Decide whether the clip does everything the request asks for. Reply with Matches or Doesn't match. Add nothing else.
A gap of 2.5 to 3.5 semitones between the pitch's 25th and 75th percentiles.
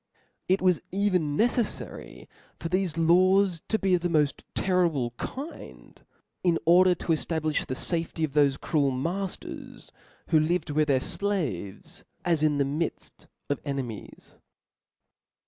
Doesn't match